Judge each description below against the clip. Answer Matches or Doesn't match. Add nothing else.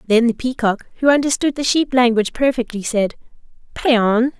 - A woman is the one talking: Matches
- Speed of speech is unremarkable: Matches